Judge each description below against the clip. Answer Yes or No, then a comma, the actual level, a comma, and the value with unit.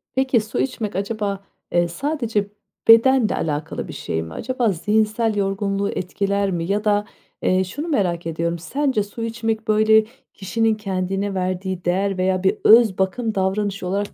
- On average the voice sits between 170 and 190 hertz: No, high, 200 Hz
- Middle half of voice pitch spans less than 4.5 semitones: Yes, average, 3.0 semitones